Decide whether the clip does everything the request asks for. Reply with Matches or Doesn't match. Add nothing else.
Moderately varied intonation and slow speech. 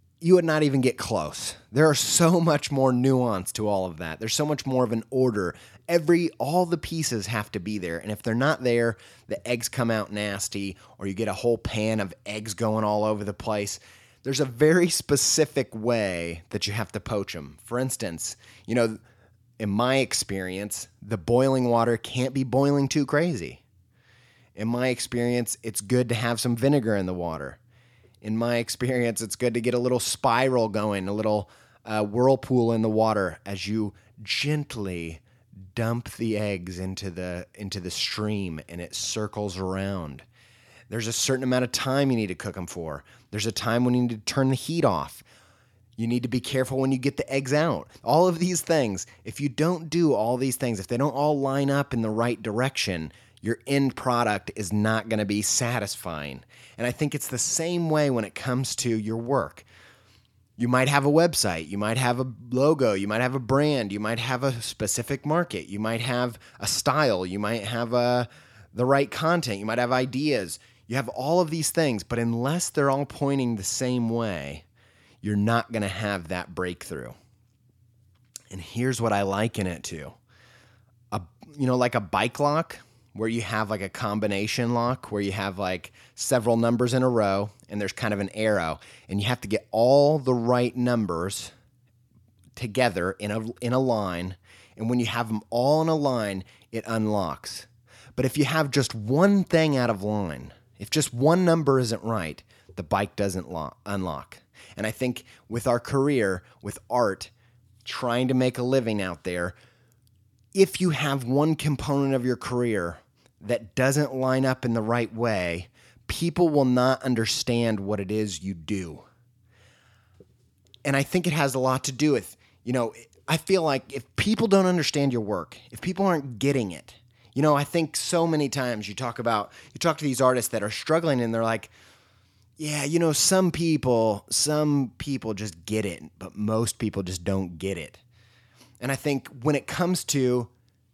Doesn't match